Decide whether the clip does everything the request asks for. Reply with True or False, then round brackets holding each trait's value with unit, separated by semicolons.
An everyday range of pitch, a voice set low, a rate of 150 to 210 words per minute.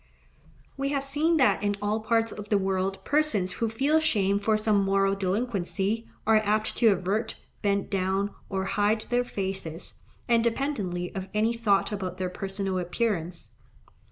False (3.0 semitones; 205 Hz; 155 wpm)